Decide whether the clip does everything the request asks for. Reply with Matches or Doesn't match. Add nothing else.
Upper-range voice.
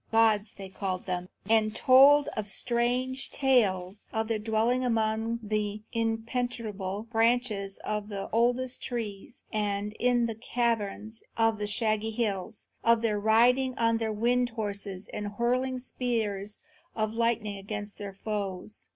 Matches